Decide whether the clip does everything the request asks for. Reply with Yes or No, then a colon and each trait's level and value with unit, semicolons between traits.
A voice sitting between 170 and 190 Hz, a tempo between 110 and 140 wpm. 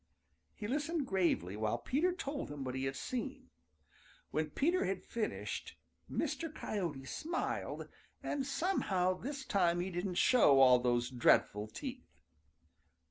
Yes: medium, 185 Hz; slow, 135 wpm